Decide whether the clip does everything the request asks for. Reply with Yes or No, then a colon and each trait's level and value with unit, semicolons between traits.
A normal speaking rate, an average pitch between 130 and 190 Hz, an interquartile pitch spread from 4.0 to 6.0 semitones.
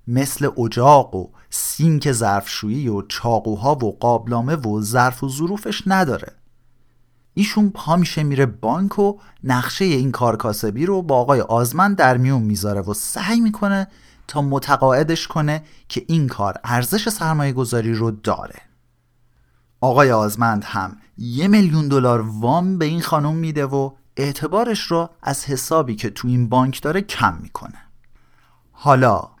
Yes: average, 140 wpm; low, 135 Hz; average, 5.2 semitones